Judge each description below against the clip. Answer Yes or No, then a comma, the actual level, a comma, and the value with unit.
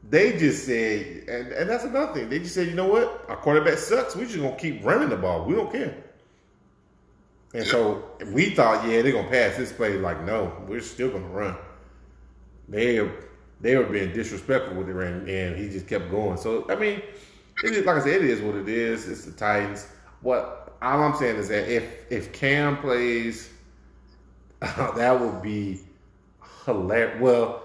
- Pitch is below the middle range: Yes, low, 110 Hz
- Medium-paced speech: Yes, average, 190 wpm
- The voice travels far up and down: Yes, wide, 5.8 semitones